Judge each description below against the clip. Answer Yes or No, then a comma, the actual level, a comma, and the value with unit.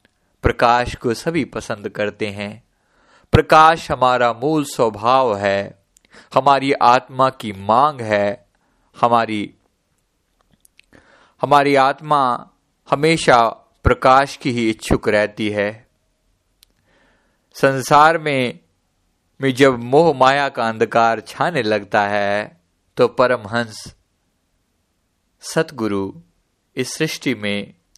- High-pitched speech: No, low, 115 Hz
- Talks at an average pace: No, slow, 90 wpm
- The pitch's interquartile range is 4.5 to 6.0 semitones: Yes, average, 4.8 semitones